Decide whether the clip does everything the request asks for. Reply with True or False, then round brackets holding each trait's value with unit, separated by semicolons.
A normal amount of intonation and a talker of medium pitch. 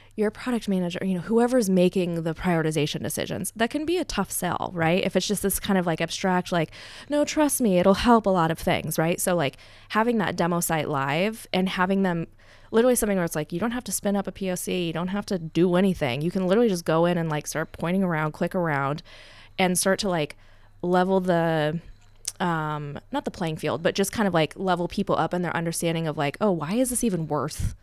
True (3.7 semitones; 180 Hz)